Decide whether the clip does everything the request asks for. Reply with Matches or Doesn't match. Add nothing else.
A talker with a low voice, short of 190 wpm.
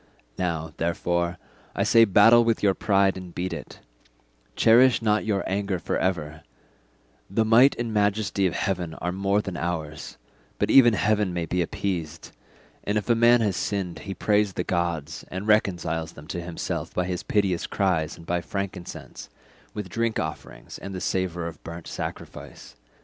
Matches